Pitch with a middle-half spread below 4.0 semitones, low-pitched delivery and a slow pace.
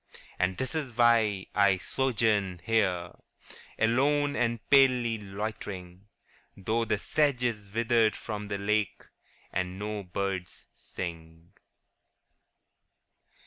Yes: average, 3.6 semitones; low, 105 Hz; slow, 105 wpm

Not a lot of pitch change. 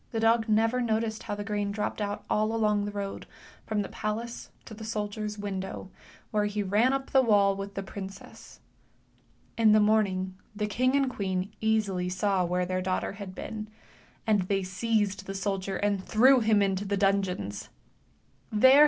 Yes: narrow, 2.0 semitones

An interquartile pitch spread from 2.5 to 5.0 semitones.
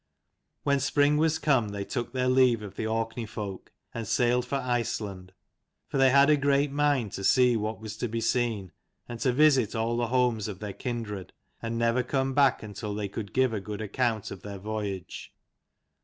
Yes: average, 3.6 semitones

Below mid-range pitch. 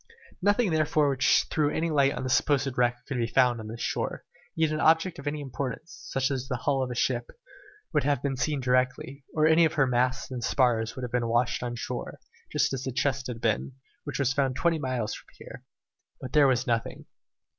Yes: low, 130 Hz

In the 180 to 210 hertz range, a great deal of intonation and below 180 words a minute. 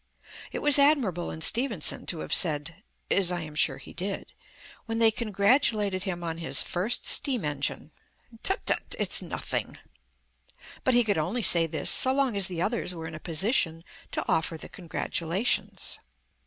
Yes: medium, 185 Hz; wide, 5.9 semitones; average, 170 wpm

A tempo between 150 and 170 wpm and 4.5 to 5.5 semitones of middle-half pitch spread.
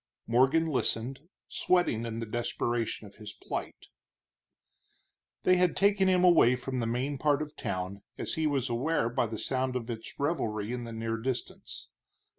Yes: average, 165 wpm; average, 5.0 semitones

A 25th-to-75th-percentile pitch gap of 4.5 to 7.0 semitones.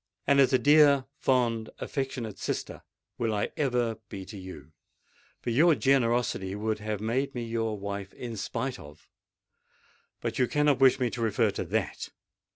No: average, 3.9 semitones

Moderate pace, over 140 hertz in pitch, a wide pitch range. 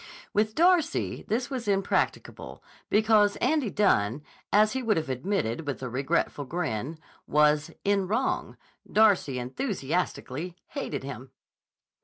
No: slow, 120 wpm; medium, 185 Hz; wide, 7.7 semitones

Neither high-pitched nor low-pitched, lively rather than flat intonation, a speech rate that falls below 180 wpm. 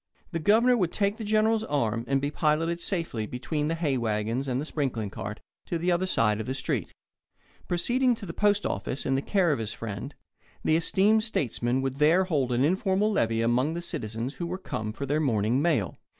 No: medium, 150 Hz; wide, 7.4 semitones; fast, 205 wpm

